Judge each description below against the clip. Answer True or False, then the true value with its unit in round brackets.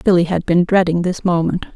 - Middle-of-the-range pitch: True (175 Hz)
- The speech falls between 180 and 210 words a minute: True (205 wpm)